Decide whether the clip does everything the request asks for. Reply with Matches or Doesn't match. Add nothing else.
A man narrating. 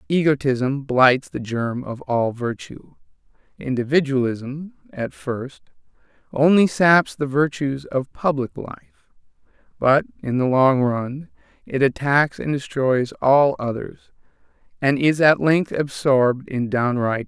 Matches